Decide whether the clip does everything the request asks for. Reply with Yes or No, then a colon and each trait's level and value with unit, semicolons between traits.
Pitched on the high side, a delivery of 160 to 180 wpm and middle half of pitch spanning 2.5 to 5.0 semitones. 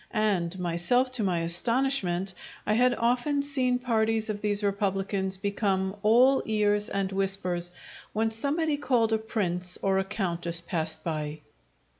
No: high, 205 Hz; average, 140 wpm; average, 4.3 semitones